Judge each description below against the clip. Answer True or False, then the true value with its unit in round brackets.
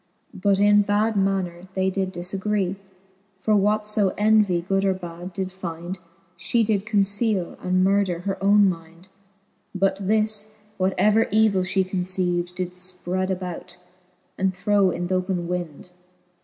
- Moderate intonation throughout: False (2.2 semitones)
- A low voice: False (190 Hz)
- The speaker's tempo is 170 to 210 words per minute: False (145 wpm)